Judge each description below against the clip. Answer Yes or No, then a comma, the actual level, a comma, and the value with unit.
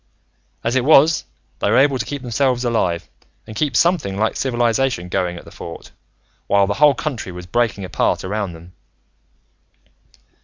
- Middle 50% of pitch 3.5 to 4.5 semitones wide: No, wide, 5.6 semitones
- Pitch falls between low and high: No, low, 115 Hz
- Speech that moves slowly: No, average, 160 wpm